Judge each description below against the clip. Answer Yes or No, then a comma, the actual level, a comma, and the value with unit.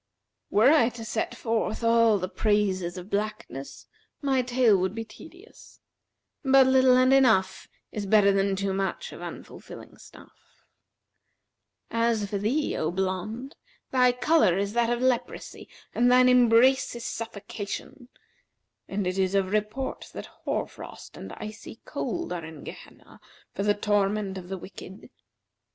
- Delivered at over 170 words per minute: No, average, 145 wpm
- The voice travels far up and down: No, average, 4.2 semitones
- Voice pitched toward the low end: No, high, 215 Hz